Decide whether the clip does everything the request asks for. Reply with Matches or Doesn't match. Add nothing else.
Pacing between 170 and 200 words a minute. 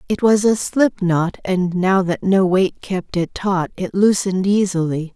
Matches